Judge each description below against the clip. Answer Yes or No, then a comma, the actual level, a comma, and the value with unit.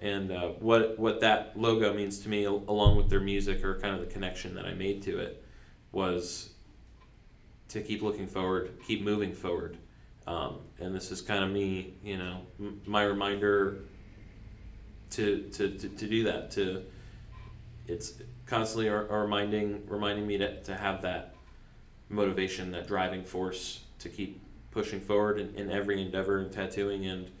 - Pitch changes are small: Yes, narrow, 1.7 semitones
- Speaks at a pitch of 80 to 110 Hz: Yes, low, 100 Hz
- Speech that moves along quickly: No, average, 165 wpm